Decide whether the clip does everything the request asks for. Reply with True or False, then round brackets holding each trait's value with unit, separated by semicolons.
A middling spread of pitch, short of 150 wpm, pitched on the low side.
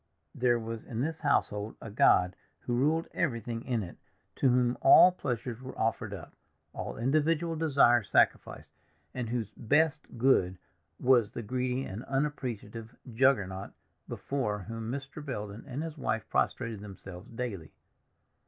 True (3.9 semitones; 140 wpm; 120 Hz)